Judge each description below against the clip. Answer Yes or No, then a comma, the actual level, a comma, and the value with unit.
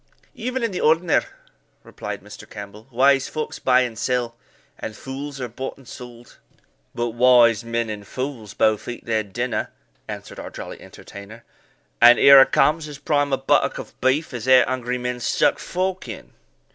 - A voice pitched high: No, low, 125 Hz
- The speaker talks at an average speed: Yes, average, 170 wpm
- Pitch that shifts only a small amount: No, average, 3.0 semitones